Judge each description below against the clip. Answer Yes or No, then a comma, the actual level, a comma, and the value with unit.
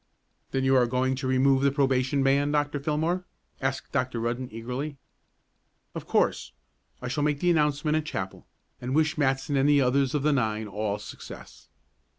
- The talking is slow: No, average, 165 wpm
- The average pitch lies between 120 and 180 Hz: Yes, low, 135 Hz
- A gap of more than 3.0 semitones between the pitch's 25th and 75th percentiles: No, narrow, 2.5 semitones